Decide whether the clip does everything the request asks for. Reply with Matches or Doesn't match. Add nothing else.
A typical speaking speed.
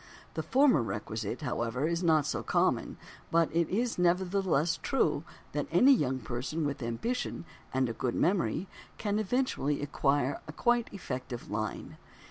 Matches